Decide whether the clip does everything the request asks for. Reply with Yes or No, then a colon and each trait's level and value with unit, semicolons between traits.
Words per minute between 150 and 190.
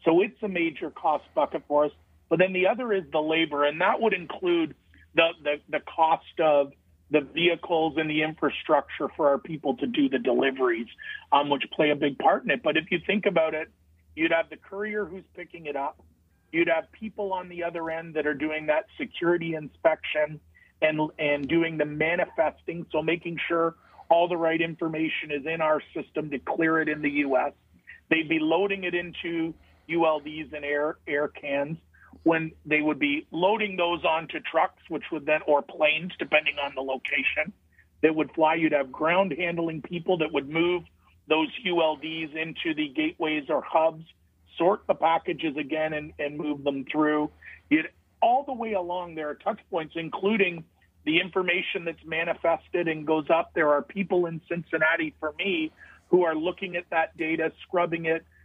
Yes: average, 185 wpm